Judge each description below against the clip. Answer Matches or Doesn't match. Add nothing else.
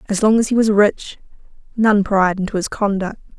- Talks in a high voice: Matches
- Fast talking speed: Doesn't match